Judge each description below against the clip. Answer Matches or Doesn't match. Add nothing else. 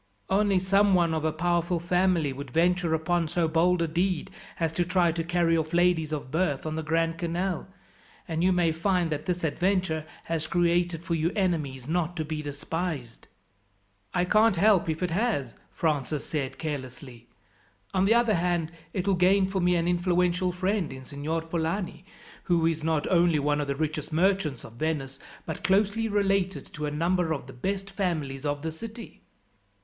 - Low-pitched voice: Doesn't match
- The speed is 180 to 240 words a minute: Matches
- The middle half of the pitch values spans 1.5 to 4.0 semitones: Matches